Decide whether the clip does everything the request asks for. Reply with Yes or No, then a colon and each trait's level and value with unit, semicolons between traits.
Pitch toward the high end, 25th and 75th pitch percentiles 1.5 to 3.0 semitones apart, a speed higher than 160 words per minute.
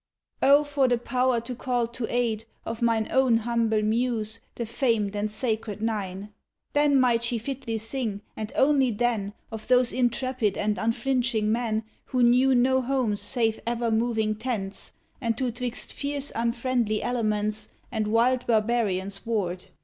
No: high, 230 Hz; average, 2.7 semitones; average, 150 wpm